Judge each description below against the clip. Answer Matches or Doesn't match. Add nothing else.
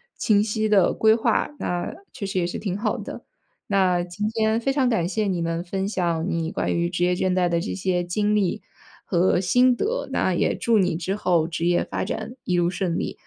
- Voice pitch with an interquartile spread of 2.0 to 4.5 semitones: Matches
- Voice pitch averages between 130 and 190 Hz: Matches